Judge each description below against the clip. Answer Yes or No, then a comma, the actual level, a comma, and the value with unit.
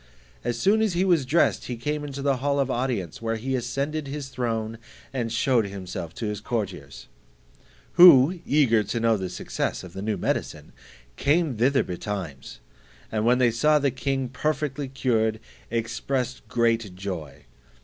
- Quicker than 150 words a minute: Yes, average, 160 wpm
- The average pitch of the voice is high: No, low, 125 Hz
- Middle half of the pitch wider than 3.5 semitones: Yes, average, 4.2 semitones